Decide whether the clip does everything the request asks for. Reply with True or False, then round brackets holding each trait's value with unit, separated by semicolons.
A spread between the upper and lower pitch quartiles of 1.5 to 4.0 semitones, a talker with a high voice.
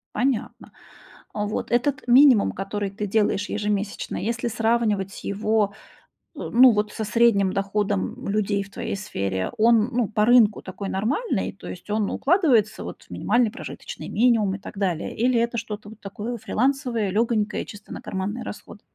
True (2.8 semitones; 215 Hz)